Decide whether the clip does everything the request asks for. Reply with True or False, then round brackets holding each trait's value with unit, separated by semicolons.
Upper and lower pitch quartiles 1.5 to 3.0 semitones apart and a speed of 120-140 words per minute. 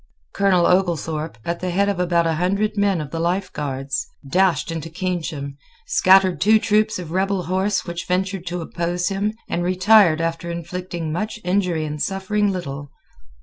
False (2.7 semitones; 165 wpm)